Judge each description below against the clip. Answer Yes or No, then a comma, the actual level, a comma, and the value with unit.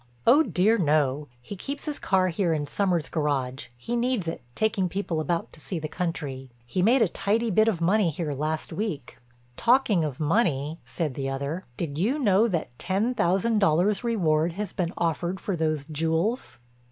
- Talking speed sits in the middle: Yes, average, 175 wpm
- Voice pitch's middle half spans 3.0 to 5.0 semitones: No, wide, 5.4 semitones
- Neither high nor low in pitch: Yes, medium, 175 Hz